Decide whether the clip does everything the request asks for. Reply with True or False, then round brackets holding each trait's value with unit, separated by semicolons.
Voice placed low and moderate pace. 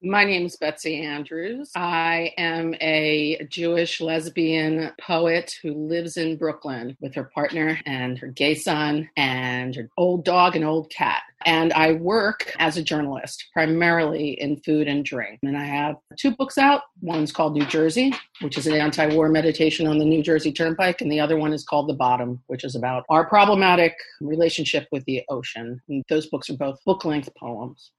False (155 Hz; 180 wpm)